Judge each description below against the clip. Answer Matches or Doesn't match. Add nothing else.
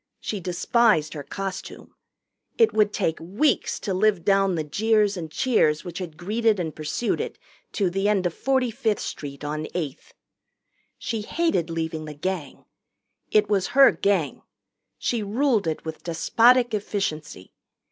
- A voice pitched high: Matches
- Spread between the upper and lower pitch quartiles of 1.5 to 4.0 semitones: Doesn't match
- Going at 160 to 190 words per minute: Doesn't match